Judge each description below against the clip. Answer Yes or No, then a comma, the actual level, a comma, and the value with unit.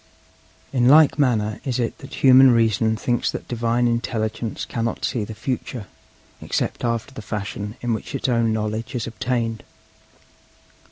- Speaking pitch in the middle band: No, low, 115 Hz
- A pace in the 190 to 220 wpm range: No, average, 150 wpm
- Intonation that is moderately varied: No, narrow, 2.2 semitones